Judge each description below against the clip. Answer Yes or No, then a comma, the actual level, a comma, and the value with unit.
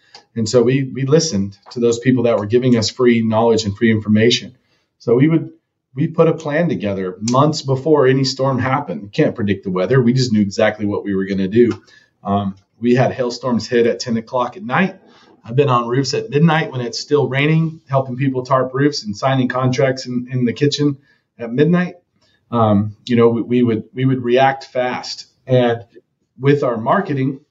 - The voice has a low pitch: Yes, low, 125 Hz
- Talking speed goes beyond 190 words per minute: Yes, average, 200 wpm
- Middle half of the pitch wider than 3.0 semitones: Yes, average, 3.4 semitones